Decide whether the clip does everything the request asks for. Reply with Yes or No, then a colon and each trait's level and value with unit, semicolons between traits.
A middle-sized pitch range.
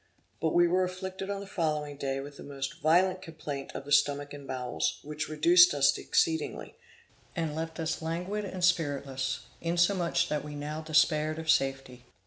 Yes: average, 3.3 semitones